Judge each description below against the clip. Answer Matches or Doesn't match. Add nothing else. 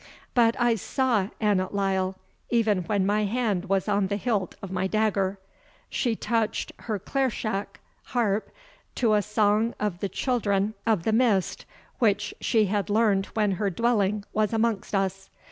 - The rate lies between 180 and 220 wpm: Doesn't match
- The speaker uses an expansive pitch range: Doesn't match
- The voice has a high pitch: Matches